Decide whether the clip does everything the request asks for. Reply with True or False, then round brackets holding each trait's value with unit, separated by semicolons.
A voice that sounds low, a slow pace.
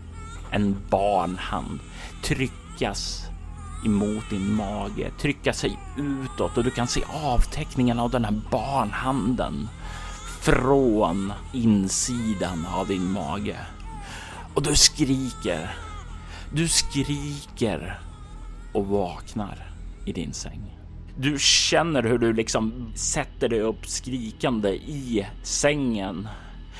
True (105 Hz; 100 wpm)